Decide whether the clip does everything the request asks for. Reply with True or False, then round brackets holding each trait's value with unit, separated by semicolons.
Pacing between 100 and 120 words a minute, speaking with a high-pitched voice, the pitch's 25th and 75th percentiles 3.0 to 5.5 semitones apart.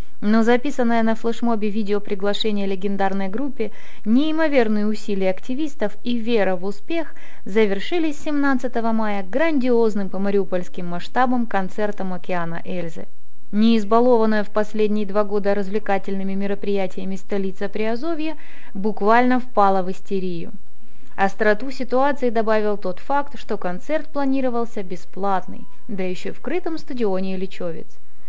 True (110 wpm; 215 Hz; 4.0 semitones)